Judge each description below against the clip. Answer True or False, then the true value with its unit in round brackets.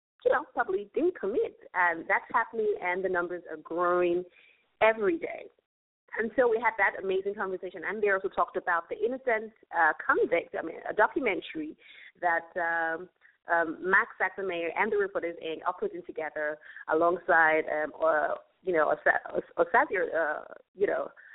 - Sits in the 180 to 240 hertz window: True (190 Hz)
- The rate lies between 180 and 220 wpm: False (165 wpm)